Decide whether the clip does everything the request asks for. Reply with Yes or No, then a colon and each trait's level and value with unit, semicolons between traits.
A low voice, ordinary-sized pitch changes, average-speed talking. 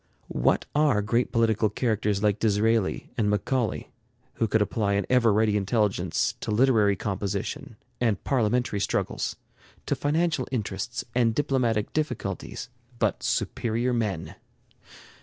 No: low, 110 Hz; average, 3.2 semitones; slow, 120 wpm